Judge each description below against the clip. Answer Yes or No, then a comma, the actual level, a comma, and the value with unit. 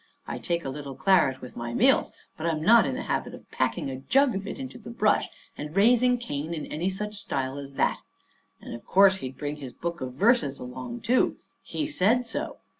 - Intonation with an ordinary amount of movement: No, wide, 8.7 semitones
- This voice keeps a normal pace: No, fast, 215 wpm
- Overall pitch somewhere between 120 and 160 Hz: No, medium, 170 Hz